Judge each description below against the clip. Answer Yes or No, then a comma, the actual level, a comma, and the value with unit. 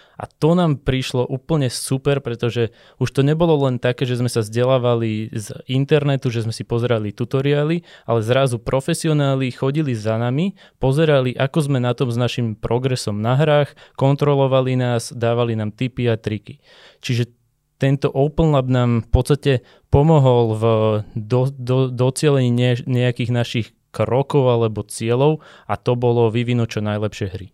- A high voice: No, low, 125 Hz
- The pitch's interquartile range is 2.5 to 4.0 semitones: Yes, average, 2.8 semitones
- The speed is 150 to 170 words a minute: Yes, average, 155 wpm